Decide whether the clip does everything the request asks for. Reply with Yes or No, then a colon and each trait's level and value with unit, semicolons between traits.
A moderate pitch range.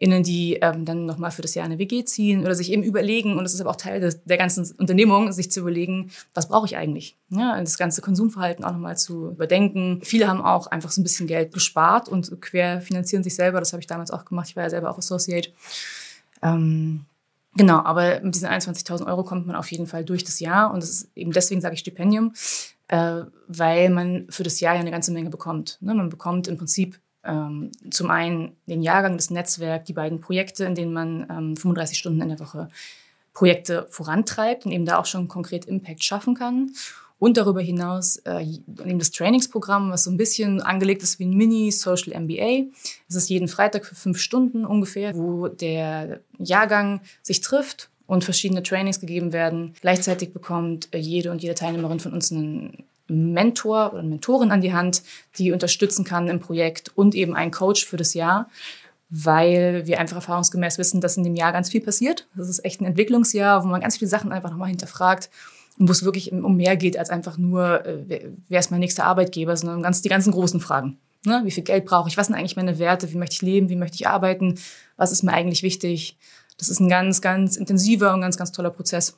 No: narrow, 2.1 semitones